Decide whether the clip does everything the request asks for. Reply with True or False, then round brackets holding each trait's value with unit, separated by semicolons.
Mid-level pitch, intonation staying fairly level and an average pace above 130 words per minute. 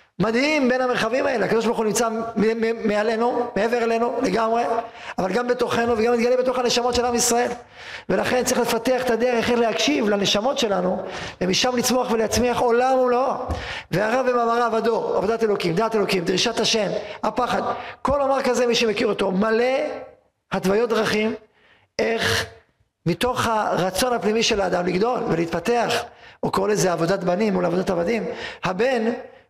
False (230 Hz; 2.3 semitones; 145 wpm)